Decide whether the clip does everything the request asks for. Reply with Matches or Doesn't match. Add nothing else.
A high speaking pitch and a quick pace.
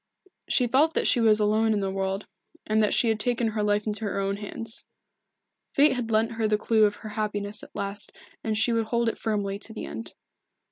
Matches